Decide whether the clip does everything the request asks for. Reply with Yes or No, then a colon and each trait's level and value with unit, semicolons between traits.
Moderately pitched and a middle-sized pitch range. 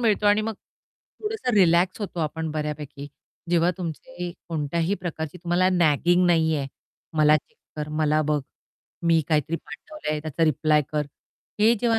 Yes: medium, 165 Hz; average, 3.1 semitones